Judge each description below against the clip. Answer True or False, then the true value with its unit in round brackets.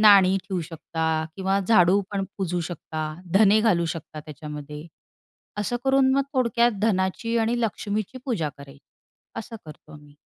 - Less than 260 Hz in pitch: True (190 Hz)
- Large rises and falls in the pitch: True (5.9 semitones)